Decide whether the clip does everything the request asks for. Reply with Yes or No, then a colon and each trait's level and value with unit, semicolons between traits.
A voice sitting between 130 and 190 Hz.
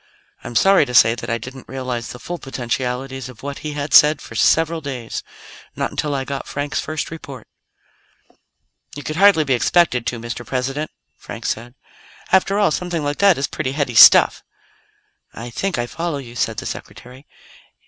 Yes: low, 135 Hz